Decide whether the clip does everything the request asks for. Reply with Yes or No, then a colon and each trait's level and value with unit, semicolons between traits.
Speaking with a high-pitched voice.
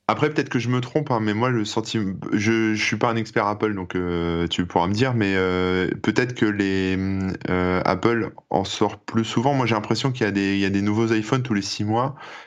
No: low, 110 Hz